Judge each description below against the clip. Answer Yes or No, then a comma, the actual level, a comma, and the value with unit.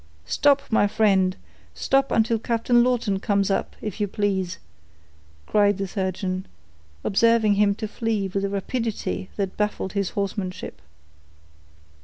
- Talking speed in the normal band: No, slow, 125 wpm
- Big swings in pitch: No, narrow, 2.5 semitones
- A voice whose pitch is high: Yes, high, 205 Hz